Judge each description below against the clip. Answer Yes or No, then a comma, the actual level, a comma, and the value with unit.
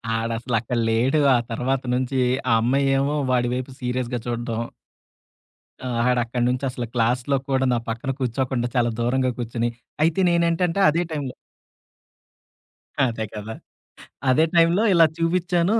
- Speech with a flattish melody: No, average, 3.2 semitones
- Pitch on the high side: No, low, 125 Hz